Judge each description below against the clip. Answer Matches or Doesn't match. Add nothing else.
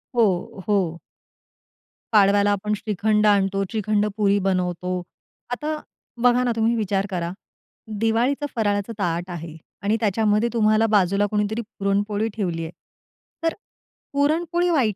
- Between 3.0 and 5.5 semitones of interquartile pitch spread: Doesn't match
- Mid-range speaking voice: Doesn't match